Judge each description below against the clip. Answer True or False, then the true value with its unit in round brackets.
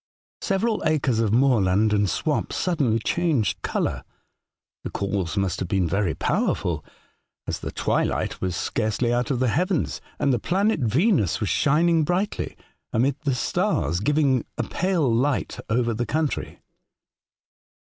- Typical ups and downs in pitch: False (6.8 semitones)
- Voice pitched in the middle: False (125 Hz)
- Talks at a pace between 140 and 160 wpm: True (145 wpm)